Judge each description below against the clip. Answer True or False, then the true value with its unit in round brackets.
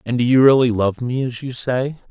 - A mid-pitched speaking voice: False (125 Hz)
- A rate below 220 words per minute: False (255 wpm)